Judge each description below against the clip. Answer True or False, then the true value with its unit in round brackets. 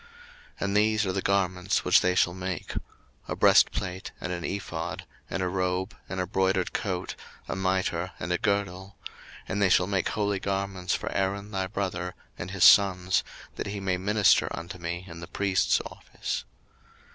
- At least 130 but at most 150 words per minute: False (175 wpm)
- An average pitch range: False (1.5 semitones)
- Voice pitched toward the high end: False (95 Hz)